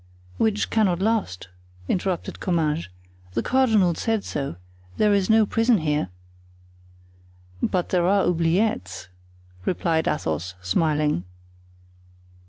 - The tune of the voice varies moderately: No, wide, 5.9 semitones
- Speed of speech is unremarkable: No, slow, 100 wpm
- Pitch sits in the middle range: Yes, medium, 175 Hz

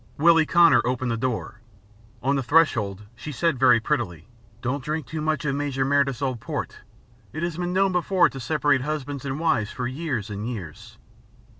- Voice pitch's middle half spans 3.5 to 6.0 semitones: Yes, average, 4.4 semitones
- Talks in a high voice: No, medium, 140 Hz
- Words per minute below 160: No, average, 185 wpm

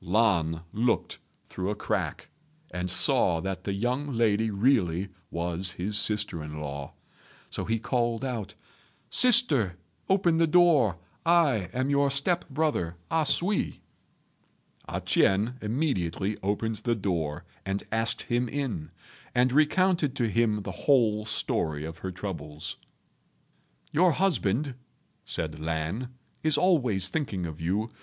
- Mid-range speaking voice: No, low, 110 Hz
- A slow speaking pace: Yes, slow, 130 wpm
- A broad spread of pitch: Yes, wide, 7.2 semitones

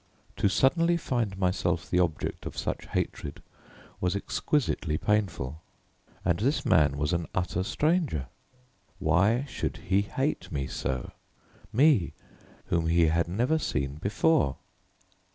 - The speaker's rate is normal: No, slow, 125 wpm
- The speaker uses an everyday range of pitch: No, wide, 7.5 semitones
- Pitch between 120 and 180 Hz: No, very low, 90 Hz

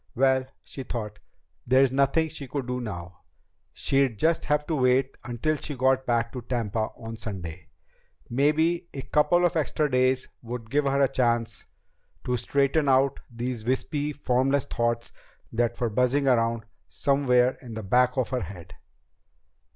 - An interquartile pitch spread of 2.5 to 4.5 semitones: Yes, average, 2.9 semitones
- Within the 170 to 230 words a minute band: No, average, 155 wpm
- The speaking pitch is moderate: No, low, 130 Hz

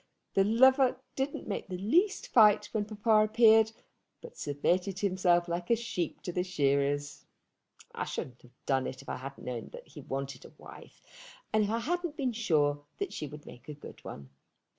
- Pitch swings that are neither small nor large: No, wide, 7.8 semitones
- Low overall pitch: No, medium, 185 Hz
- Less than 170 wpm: No, average, 185 wpm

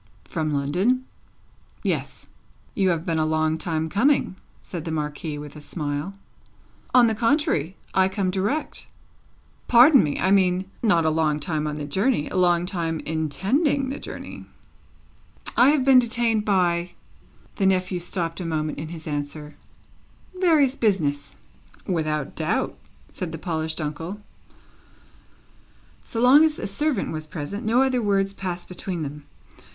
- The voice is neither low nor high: Yes, medium, 180 Hz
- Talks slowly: No, average, 145 wpm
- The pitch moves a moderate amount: No, wide, 6.0 semitones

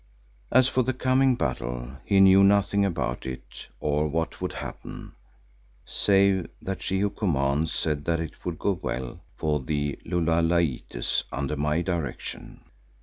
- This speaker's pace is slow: No, average, 145 wpm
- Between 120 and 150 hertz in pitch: No, very low, 80 Hz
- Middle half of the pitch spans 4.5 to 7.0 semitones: Yes, average, 5.1 semitones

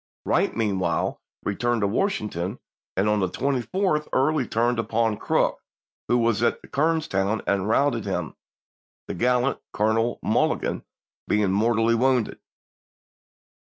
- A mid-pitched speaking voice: No, low, 115 Hz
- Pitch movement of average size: Yes, average, 3.7 semitones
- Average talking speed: No, slow, 120 wpm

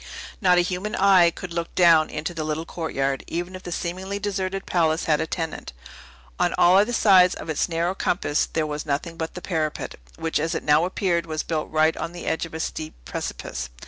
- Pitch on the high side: No, medium, 170 Hz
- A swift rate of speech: Yes, fast, 210 wpm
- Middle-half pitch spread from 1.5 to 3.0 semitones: Yes, narrow, 2.5 semitones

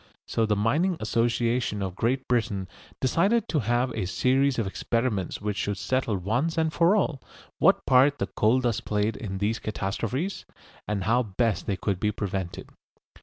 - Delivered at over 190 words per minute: No, average, 170 wpm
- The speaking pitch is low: Yes, low, 115 Hz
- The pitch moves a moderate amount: Yes, average, 4.1 semitones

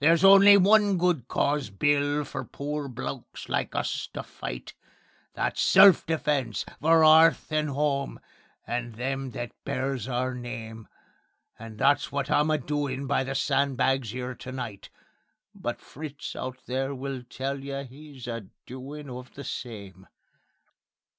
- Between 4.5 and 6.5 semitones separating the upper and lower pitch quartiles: No, average, 2.9 semitones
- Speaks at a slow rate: No, average, 145 wpm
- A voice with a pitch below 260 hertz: Yes, low, 135 Hz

